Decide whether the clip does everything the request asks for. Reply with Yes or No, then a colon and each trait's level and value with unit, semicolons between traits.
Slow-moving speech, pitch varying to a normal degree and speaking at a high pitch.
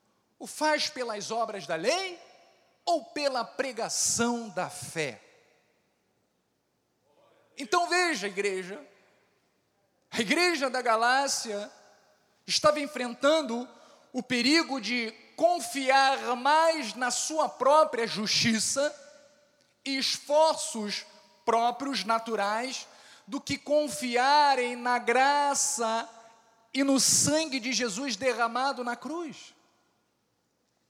Yes: slow, 90 wpm; average, 4.1 semitones; very high, 265 Hz